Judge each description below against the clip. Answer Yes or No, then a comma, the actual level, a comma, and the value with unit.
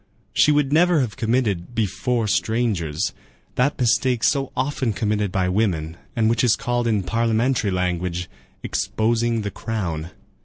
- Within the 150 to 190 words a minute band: No, average, 140 wpm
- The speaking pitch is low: Yes, low, 110 Hz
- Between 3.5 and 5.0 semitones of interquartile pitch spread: Yes, average, 4.4 semitones